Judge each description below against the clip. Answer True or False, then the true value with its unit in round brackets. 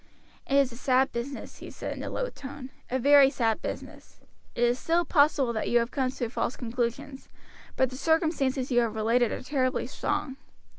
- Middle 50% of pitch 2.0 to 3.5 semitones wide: True (2.8 semitones)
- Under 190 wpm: False (200 wpm)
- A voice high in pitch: True (260 Hz)